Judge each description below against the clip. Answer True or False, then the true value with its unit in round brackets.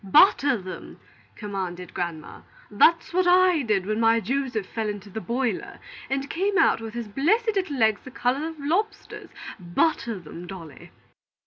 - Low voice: False (230 Hz)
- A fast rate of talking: False (155 wpm)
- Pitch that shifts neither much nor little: False (8.1 semitones)